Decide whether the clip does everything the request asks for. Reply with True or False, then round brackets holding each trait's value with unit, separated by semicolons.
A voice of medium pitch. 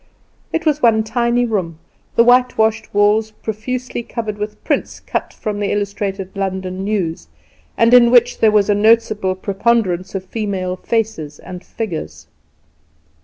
False (210 Hz)